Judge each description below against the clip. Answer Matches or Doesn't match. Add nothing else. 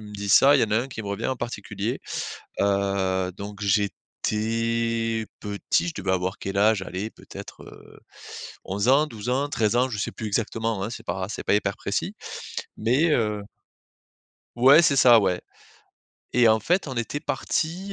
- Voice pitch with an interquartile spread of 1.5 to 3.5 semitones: Doesn't match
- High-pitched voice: Doesn't match